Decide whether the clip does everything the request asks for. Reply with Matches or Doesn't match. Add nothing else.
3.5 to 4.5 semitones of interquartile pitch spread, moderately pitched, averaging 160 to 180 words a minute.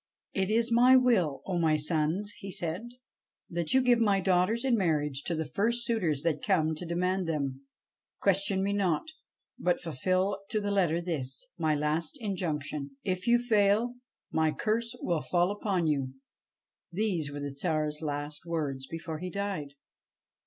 Doesn't match